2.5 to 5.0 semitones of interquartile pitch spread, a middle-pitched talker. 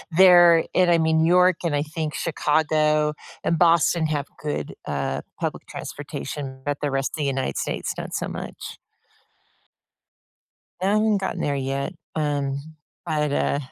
Yes: average, 2.9 semitones; medium, 155 Hz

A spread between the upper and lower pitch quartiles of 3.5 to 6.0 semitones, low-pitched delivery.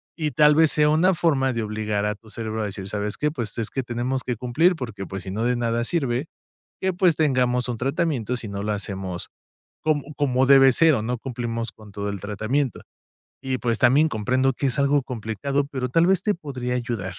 Yes: average, 4.7 semitones; low, 125 Hz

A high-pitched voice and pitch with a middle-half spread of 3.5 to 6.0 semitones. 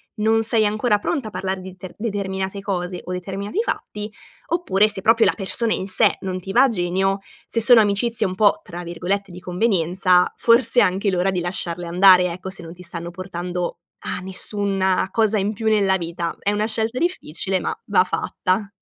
No: high, 195 Hz; average, 2.9 semitones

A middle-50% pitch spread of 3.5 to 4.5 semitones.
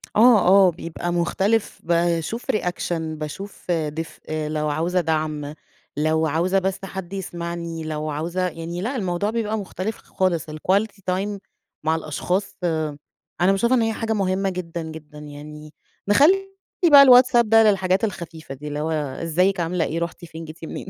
Yes: average, 3.8 semitones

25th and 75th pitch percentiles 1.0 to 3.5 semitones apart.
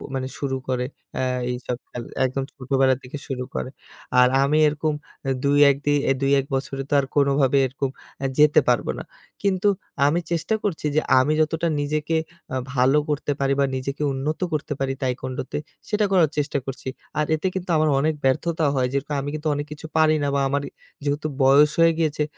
Yes: narrow, 2.4 semitones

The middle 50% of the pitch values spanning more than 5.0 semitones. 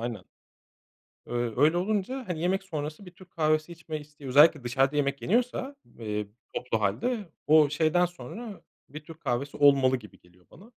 Yes: wide, 5.6 semitones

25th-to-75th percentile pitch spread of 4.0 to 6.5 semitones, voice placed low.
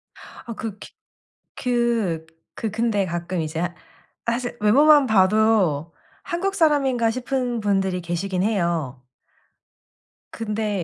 No: average, 5.1 semitones; high, 215 Hz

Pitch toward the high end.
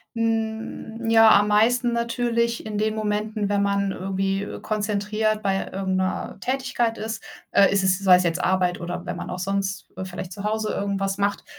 Yes: high, 205 Hz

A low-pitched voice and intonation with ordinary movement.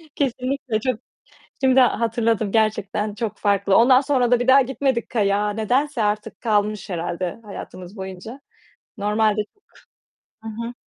No: high, 220 Hz; average, 3.5 semitones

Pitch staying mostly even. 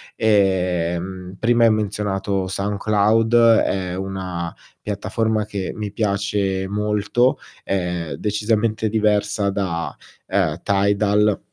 Yes: narrow, 2.0 semitones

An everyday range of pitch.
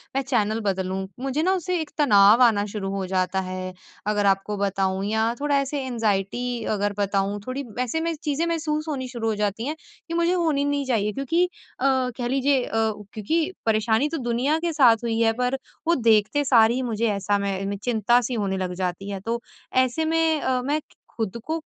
No: wide, 5.9 semitones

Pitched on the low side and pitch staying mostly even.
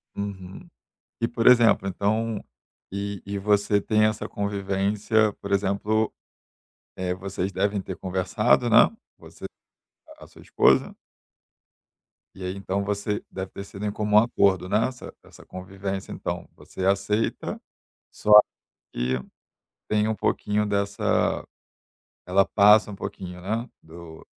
Yes: low, 100 Hz; narrow, 1.7 semitones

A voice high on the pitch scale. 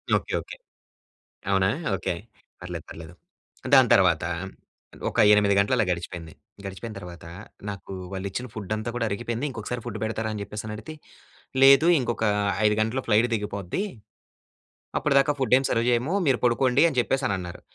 No: low, 110 Hz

